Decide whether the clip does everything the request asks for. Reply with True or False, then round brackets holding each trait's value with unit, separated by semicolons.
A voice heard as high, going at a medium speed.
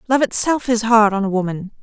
False (220 Hz; 230 wpm)